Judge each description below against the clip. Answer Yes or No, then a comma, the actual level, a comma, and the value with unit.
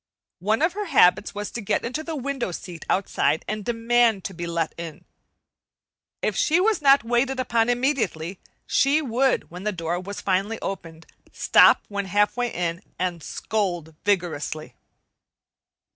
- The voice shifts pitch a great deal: Yes, wide, 5.9 semitones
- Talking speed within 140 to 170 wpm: Yes, average, 150 wpm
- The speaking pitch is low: No, high, 205 Hz